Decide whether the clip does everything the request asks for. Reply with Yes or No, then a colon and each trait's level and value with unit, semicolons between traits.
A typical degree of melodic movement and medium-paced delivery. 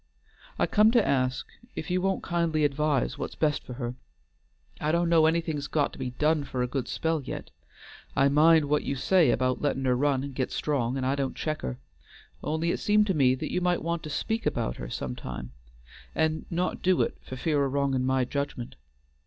No: average, 3.9 semitones; fast, 210 wpm